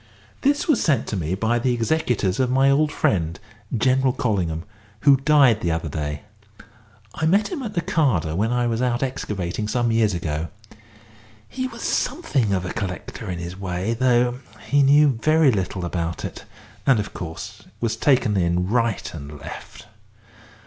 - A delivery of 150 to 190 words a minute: Yes, average, 165 wpm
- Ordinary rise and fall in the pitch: No, wide, 7.1 semitones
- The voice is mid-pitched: No, low, 115 Hz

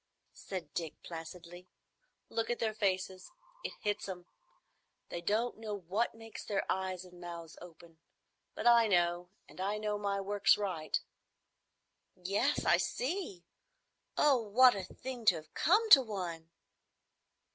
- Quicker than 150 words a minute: No, average, 140 wpm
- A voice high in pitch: Yes, high, 195 Hz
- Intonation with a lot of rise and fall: No, average, 4.1 semitones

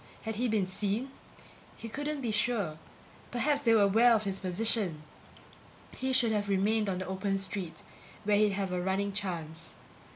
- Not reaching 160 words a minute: No, average, 170 wpm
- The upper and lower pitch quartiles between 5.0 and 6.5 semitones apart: No, average, 3.1 semitones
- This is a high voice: Yes, high, 205 Hz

